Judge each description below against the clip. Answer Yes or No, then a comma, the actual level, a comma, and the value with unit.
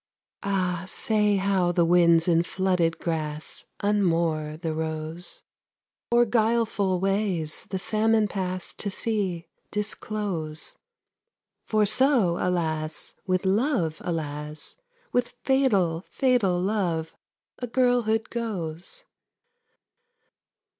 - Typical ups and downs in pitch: Yes, average, 4.6 semitones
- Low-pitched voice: No, medium, 185 Hz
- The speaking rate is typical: No, slow, 90 wpm